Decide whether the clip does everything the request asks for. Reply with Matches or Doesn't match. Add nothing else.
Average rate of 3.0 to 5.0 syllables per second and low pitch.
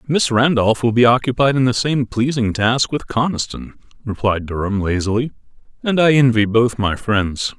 Matches